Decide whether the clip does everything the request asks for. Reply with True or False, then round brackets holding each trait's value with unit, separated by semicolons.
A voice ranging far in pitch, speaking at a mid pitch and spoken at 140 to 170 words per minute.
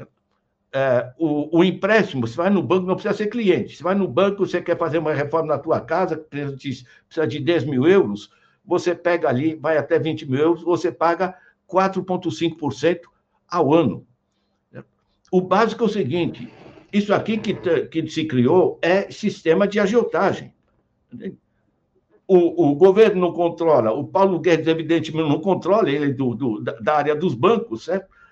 False (3.5 semitones; 170 Hz; 160 wpm)